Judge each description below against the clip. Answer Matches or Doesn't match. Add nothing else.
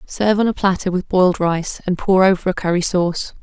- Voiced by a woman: Matches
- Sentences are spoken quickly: Matches